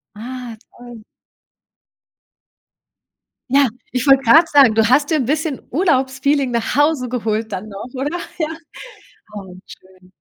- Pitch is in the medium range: No, very high, 255 Hz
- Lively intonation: No, average, 4.4 semitones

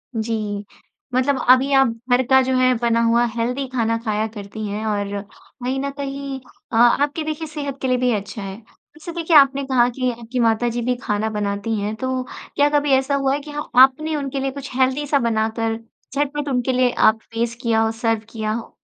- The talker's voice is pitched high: Yes, very high, 250 Hz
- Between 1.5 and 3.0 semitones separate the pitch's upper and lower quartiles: No, average, 3.5 semitones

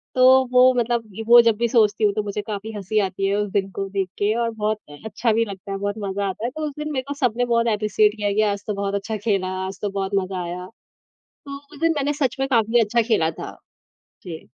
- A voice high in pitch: Yes, high, 215 Hz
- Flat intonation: No, average, 3.0 semitones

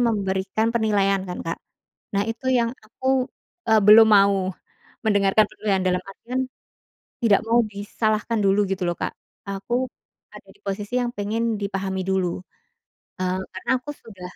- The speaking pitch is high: Yes, high, 205 Hz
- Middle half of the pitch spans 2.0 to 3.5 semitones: Yes, average, 2.9 semitones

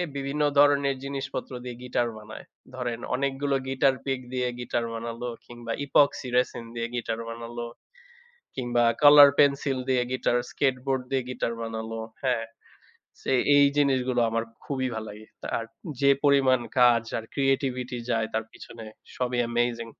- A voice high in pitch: No, low, 125 Hz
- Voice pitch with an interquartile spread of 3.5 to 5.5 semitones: No, narrow, 2.5 semitones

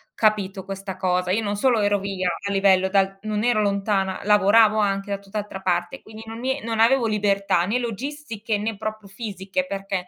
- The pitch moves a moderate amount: No, narrow, 2.2 semitones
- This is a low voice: No, high, 205 Hz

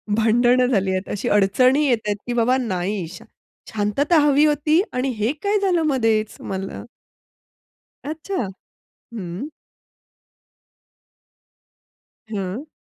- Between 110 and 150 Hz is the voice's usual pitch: No, high, 235 Hz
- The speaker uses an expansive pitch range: Yes, wide, 5.8 semitones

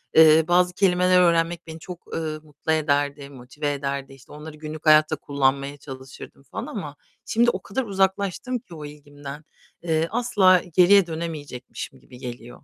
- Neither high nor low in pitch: Yes, medium, 155 Hz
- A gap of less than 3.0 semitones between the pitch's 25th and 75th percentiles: No, average, 3.9 semitones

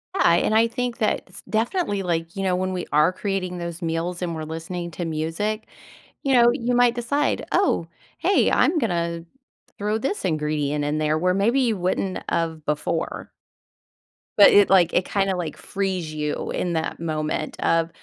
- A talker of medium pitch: Yes, medium, 180 Hz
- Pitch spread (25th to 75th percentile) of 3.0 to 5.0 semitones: Yes, average, 4.6 semitones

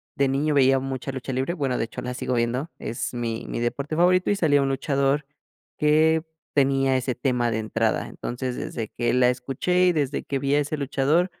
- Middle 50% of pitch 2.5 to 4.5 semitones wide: Yes, average, 2.9 semitones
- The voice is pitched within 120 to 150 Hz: Yes, low, 135 Hz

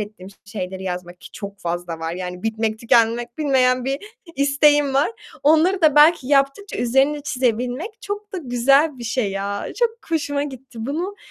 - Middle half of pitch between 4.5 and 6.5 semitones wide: Yes, wide, 5.6 semitones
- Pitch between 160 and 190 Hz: No, very high, 255 Hz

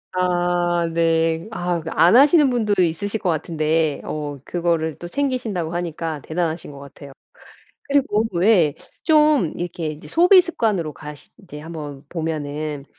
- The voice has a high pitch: No, medium, 170 Hz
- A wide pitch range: No, average, 4.5 semitones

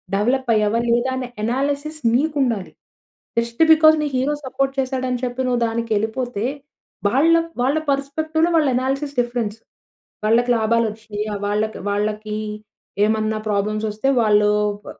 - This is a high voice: Yes, high, 240 Hz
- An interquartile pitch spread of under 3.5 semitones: No, average, 4.0 semitones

